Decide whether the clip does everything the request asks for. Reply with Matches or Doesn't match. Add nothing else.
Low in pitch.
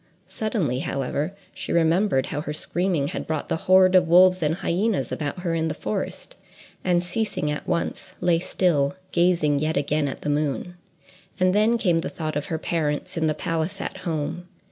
Doesn't match